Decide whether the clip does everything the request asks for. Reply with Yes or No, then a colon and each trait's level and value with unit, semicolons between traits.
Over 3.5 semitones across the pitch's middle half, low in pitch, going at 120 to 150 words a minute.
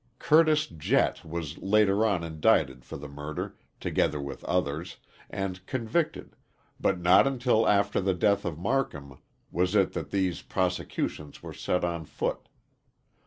Yes: average, 4.7 semitones; very low, 90 Hz; average, 140 wpm